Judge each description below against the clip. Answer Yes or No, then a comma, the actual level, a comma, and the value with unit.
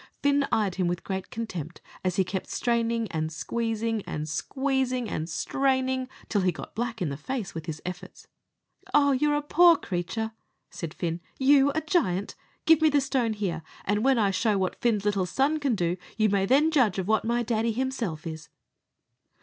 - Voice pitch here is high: Yes, high, 220 Hz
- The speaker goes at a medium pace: Yes, average, 190 wpm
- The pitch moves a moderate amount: No, wide, 6.3 semitones